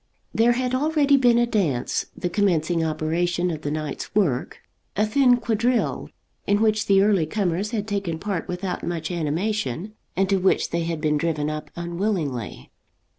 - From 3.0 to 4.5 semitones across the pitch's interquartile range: No, average, 4.9 semitones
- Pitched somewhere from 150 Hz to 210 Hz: Yes, medium, 185 Hz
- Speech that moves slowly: No, average, 165 wpm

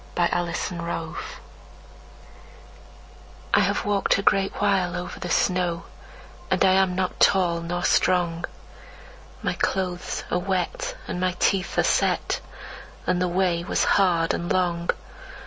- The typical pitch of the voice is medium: Yes, medium, 180 Hz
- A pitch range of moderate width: No, narrow, 1.6 semitones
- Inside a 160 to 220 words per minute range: No, average, 140 wpm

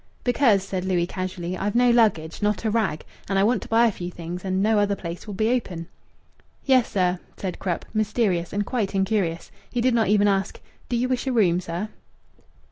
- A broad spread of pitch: No, average, 3.9 semitones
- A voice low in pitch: No, high, 200 Hz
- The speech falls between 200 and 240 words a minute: Yes, fast, 205 wpm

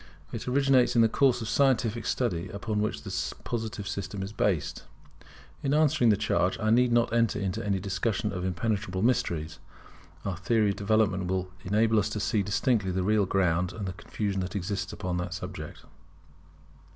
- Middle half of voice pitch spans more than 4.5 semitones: No, average, 3.4 semitones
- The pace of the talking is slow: No, average, 175 wpm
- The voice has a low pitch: Yes, low, 105 Hz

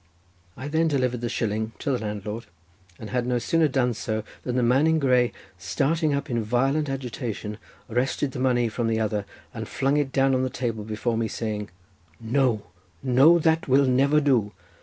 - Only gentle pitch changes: No, average, 3.5 semitones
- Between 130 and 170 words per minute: No, average, 185 wpm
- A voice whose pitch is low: Yes, low, 125 Hz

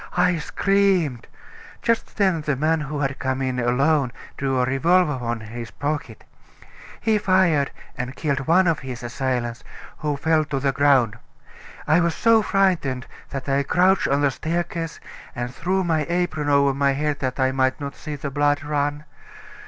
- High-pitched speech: No, medium, 145 Hz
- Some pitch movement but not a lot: Yes, average, 4.0 semitones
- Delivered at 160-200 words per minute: Yes, average, 170 wpm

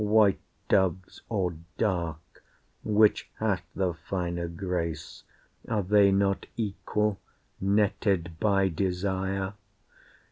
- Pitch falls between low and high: No, very low, 95 Hz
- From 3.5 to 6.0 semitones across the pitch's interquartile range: No, narrow, 2.6 semitones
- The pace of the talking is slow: Yes, slow, 95 wpm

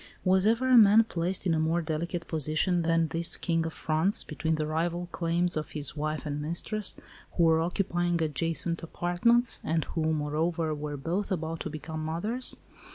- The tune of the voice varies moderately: No, narrow, 2.1 semitones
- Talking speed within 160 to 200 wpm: Yes, average, 170 wpm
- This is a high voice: No, medium, 165 Hz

